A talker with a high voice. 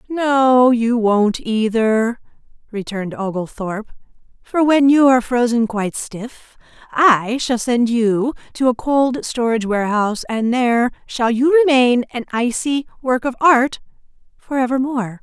Yes: high, 240 Hz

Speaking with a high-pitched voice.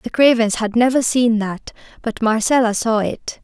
Yes: high, 230 Hz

